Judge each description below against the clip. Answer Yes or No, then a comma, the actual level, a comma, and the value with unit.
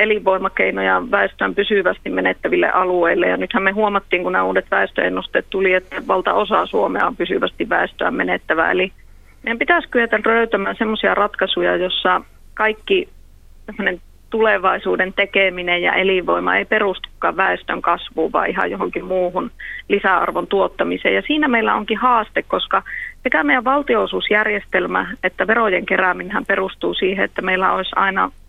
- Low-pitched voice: No, high, 200 Hz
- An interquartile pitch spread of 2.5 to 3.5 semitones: Yes, average, 3.2 semitones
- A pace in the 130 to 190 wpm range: Yes, average, 135 wpm